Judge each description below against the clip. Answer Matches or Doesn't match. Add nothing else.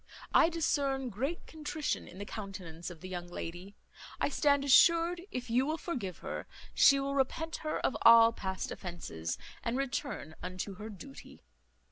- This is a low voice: Doesn't match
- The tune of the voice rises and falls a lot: Matches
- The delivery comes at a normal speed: Matches